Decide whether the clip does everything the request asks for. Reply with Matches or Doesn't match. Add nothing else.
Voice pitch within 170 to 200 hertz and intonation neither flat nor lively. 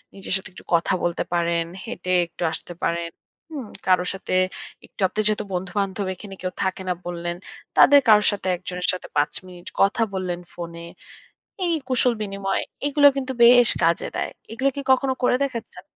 Matches